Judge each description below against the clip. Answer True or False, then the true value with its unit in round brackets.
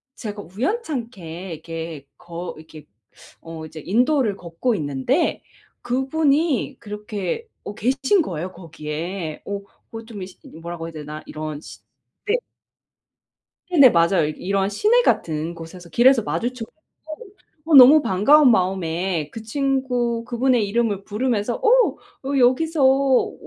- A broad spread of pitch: True (7.8 semitones)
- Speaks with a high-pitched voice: True (205 Hz)